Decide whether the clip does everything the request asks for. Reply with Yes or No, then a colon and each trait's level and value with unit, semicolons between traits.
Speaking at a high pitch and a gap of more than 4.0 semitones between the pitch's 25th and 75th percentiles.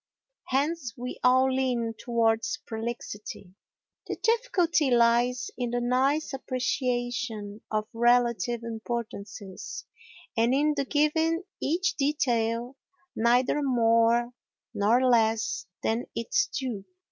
No: high, 245 Hz; average, 2.9 semitones